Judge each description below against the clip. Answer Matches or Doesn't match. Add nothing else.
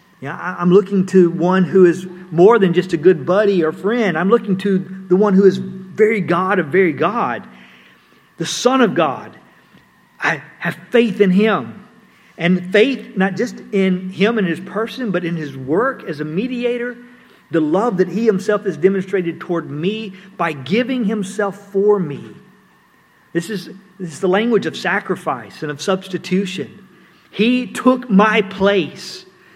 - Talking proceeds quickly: Doesn't match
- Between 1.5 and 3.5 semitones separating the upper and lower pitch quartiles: Matches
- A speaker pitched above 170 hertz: Matches